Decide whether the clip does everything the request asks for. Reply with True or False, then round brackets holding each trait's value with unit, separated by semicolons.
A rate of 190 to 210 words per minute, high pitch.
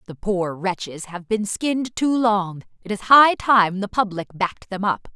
True (200 wpm; 205 Hz)